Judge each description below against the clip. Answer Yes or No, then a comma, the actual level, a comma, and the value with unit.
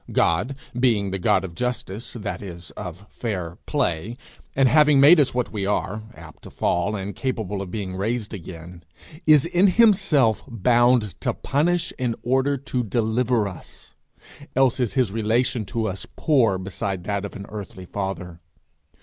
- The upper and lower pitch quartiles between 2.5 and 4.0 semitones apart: No, average, 5.0 semitones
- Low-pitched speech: Yes, low, 110 Hz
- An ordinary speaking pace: Yes, average, 160 wpm